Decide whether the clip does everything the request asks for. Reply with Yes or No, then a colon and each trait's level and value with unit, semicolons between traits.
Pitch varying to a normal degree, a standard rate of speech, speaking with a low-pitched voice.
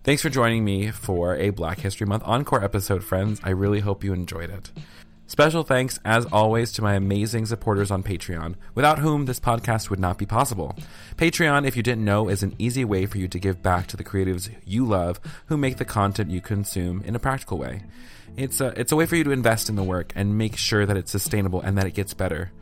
No: average, 3.8 semitones; fast, 235 wpm; low, 105 Hz